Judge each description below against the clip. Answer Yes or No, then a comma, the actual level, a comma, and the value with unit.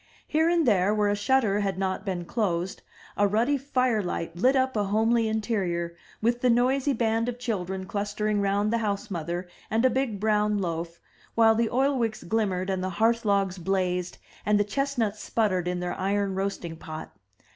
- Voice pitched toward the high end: Yes, high, 205 Hz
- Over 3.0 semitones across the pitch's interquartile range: Yes, average, 3.6 semitones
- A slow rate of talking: No, average, 180 wpm